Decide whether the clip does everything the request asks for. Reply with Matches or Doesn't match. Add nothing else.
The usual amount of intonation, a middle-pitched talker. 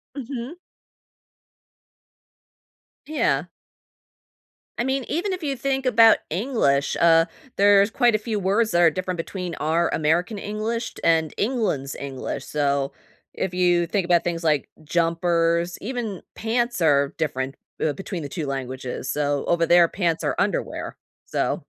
Doesn't match